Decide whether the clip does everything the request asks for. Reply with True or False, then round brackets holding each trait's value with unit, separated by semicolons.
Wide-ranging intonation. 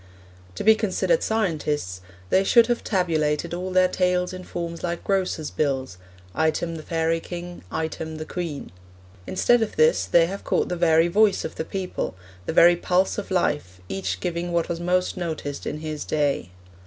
False (2.8 semitones)